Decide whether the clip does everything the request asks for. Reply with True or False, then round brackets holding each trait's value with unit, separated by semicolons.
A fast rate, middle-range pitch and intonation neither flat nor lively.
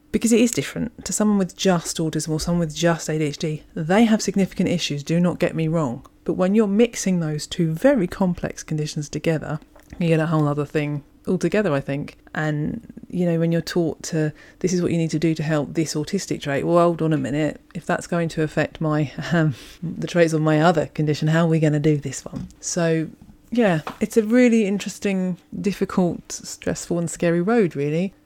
True (210 wpm; 170 Hz; 3.8 semitones)